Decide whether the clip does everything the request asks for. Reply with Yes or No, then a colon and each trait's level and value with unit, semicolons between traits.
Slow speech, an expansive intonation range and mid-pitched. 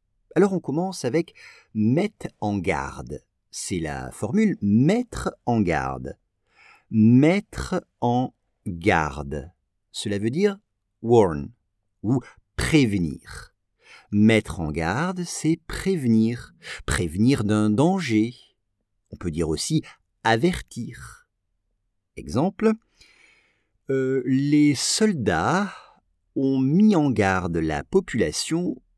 No: slow, 95 wpm; wide, 7.8 semitones; low, 110 Hz